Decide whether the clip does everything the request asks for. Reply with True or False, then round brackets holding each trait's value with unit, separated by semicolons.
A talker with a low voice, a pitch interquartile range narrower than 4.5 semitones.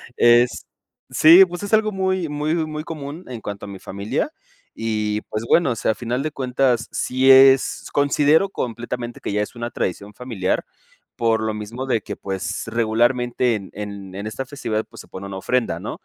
False (120 Hz; 4.9 semitones)